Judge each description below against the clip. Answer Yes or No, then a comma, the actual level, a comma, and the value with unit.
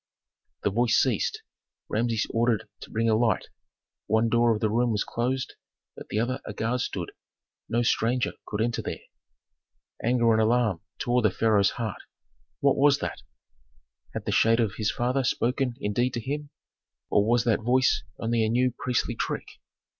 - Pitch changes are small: Yes, narrow, 2.0 semitones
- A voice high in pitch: No, low, 115 Hz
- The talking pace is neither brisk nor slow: Yes, average, 170 wpm